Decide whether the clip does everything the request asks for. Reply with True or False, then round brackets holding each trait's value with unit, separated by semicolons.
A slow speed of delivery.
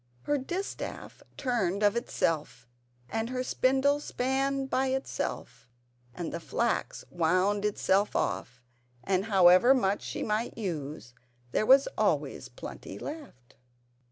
True (120 wpm)